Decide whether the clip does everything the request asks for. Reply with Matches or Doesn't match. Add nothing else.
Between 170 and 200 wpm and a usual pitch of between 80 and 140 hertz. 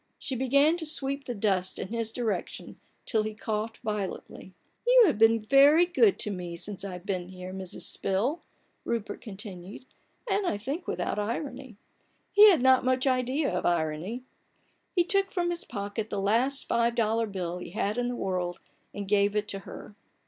Doesn't match